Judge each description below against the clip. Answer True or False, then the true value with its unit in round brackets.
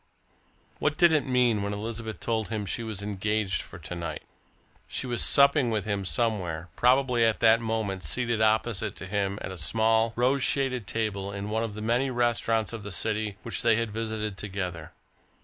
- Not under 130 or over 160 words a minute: False (185 wpm)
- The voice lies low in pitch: True (110 Hz)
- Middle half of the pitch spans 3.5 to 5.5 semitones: False (2.7 semitones)